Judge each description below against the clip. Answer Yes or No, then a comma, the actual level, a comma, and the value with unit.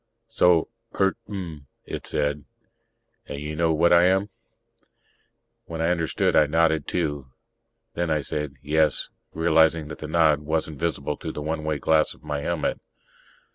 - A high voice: No, very low, 80 Hz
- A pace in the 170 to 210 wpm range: No, average, 155 wpm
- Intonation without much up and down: Yes, narrow, 1.9 semitones